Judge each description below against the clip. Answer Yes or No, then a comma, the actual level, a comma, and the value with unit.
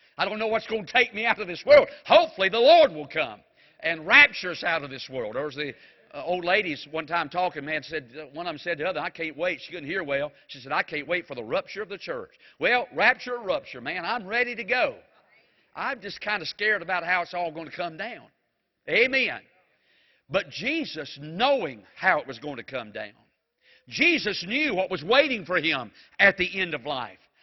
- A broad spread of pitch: Yes, wide, 7.1 semitones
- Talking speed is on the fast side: Yes, fast, 230 wpm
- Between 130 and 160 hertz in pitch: No, high, 190 Hz